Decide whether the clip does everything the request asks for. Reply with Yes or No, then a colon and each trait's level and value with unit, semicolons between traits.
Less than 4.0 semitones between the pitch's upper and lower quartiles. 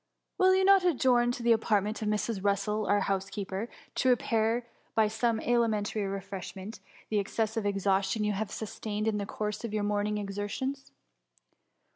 Yes: narrow, 2.4 semitones